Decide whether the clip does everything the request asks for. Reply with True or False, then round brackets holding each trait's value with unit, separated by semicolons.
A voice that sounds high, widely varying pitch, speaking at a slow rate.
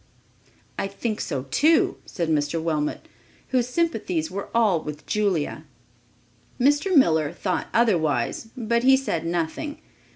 True (195 Hz; 7.3 semitones; 125 wpm)